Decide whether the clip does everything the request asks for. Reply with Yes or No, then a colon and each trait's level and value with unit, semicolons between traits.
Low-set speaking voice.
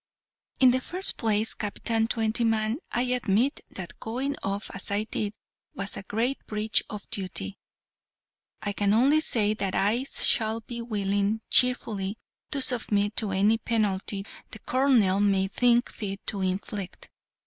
No: high, 215 Hz